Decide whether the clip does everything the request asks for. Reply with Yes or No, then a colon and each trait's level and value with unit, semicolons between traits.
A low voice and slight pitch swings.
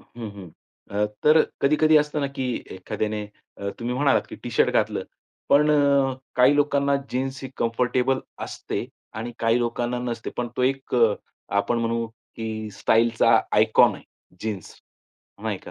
No: low, 120 Hz; average, 3.2 semitones